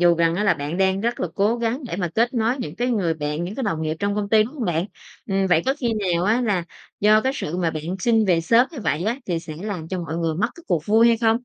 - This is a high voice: Yes, high, 195 Hz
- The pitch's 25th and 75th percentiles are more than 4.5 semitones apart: Yes, average, 5.1 semitones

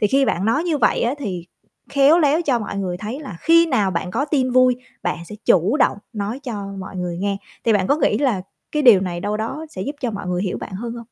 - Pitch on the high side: Yes, high, 225 Hz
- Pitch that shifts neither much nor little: No, wide, 6.3 semitones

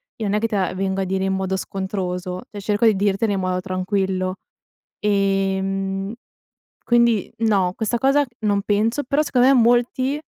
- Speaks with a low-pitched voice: No, high, 195 Hz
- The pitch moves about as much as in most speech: Yes, average, 3.0 semitones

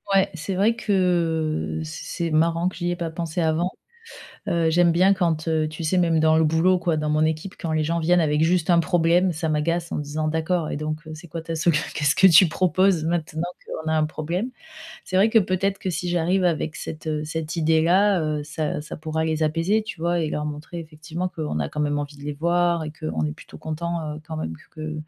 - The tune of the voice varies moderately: No, narrow, 2.1 semitones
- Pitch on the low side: No, medium, 160 Hz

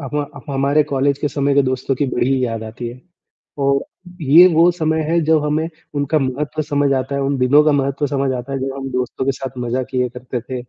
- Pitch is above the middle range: No, medium, 140 Hz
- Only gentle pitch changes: Yes, narrow, 2.2 semitones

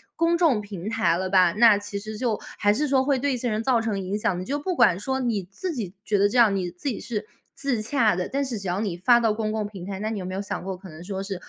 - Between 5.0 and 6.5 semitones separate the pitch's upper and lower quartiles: No, average, 4.2 semitones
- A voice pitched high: Yes, high, 215 Hz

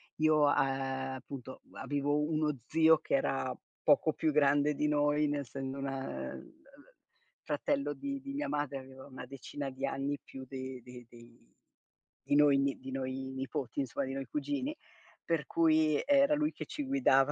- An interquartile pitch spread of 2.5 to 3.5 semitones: Yes, average, 2.8 semitones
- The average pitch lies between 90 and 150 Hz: Yes, medium, 140 Hz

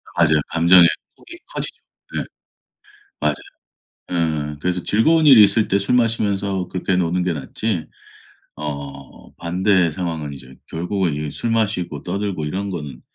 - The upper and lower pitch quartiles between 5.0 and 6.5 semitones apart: No, average, 4.5 semitones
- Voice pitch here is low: Yes, very low, 90 Hz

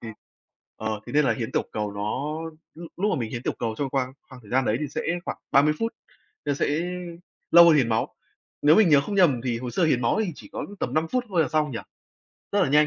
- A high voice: No, medium, 140 Hz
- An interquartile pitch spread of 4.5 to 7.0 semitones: Yes, average, 5.0 semitones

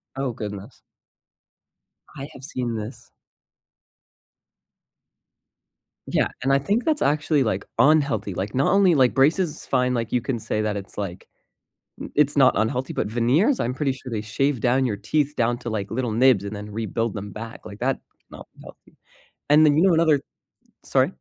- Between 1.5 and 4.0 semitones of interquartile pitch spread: No, average, 4.8 semitones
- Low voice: Yes, low, 125 Hz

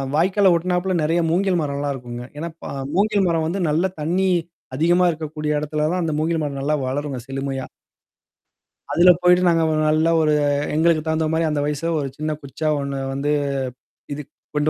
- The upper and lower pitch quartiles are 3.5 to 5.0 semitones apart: No, average, 2.9 semitones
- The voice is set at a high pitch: No, medium, 155 Hz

